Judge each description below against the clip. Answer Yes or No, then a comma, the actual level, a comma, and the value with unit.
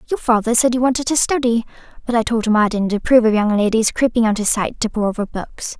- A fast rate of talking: Yes, fast, 260 wpm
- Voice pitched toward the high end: Yes, high, 230 Hz